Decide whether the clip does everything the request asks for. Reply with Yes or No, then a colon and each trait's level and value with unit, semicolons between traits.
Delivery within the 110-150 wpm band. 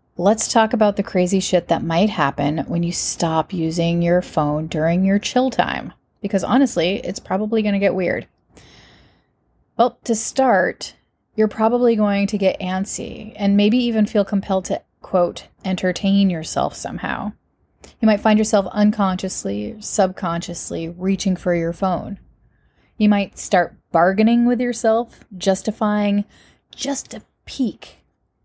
Yes: average, 140 wpm